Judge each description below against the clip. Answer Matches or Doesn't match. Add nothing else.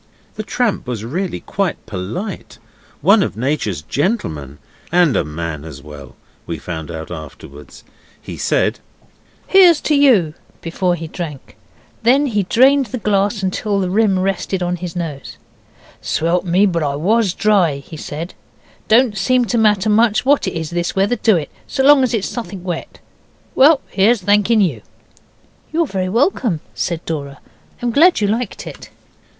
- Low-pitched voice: Doesn't match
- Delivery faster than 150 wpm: Matches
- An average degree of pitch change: Doesn't match